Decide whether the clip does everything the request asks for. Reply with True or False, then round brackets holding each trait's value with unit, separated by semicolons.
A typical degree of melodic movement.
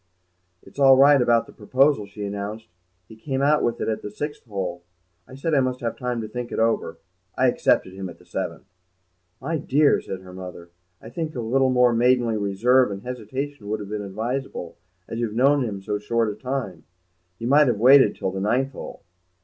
True (4.4 semitones)